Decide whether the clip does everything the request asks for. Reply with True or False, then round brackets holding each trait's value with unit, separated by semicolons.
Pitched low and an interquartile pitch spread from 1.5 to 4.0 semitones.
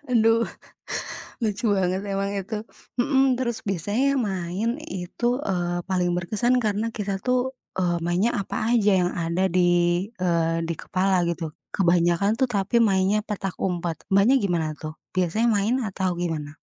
False (190 Hz; 3.6 semitones)